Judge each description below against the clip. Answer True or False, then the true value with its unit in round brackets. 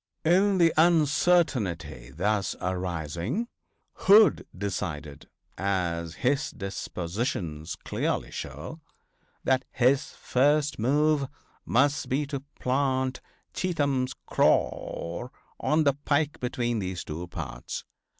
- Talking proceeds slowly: True (95 wpm)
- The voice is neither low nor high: False (125 Hz)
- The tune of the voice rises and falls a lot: True (8.5 semitones)